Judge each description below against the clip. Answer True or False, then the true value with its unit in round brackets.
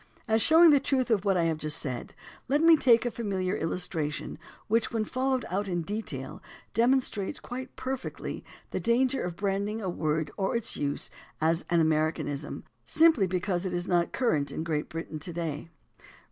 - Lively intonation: True (6.4 semitones)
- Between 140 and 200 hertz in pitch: True (190 Hz)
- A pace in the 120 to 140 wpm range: False (175 wpm)